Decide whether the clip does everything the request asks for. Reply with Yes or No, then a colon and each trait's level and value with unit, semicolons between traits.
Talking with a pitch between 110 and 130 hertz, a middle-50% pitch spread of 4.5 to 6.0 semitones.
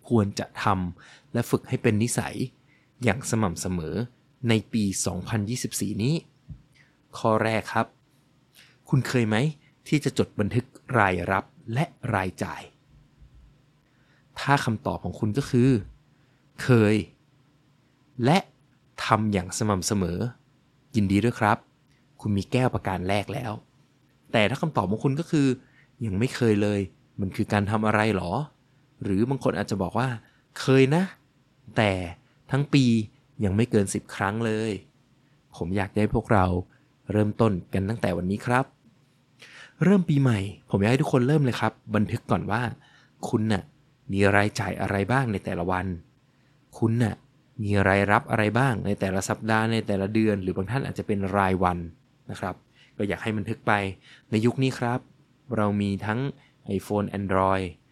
Yes: low, 115 Hz; average, 4.8 semitones